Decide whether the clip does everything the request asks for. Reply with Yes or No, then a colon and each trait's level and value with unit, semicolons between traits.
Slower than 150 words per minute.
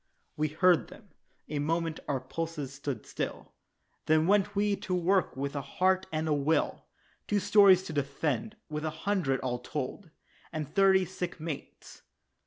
No: average, 160 wpm